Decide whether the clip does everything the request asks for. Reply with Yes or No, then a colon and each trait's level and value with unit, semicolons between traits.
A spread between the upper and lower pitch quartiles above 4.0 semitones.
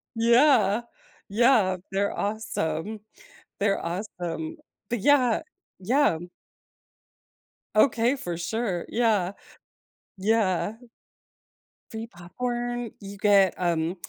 Yes: average, 4.5 semitones